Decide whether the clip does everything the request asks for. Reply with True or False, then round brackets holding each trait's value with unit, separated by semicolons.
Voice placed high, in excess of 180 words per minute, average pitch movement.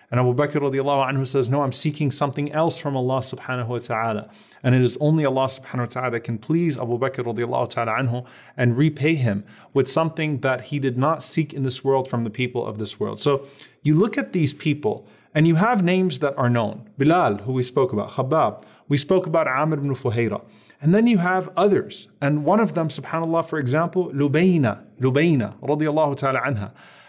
False (140 Hz; 195 wpm; 3.9 semitones)